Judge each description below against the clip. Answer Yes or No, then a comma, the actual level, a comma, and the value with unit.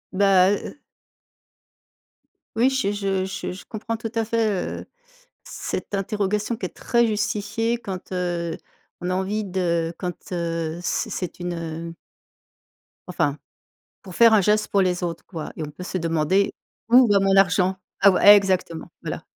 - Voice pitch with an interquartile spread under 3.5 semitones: Yes, average, 2.9 semitones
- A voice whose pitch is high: Yes, high, 195 Hz